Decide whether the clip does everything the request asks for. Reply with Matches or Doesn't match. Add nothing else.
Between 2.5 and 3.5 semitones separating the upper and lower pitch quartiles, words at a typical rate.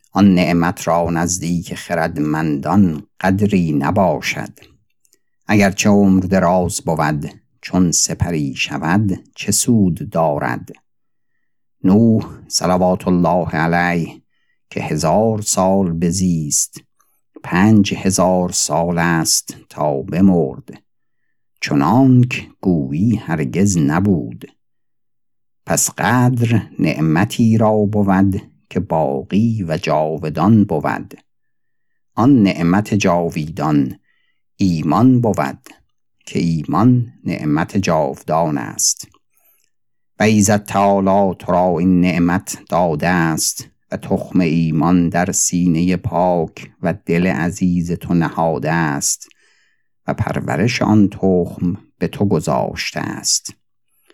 Doesn't match